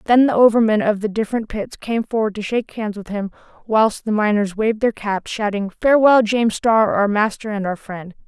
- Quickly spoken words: Yes, fast, 210 wpm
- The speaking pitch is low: No, high, 215 Hz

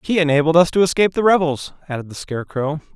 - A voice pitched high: No, medium, 160 Hz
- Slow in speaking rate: No, fast, 205 wpm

